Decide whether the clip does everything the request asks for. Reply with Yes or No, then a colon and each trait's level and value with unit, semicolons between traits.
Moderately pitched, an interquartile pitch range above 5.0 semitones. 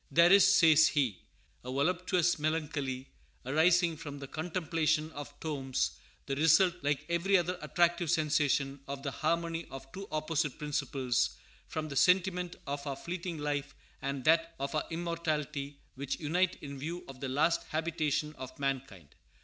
No: medium, 155 Hz; average, 3.2 semitones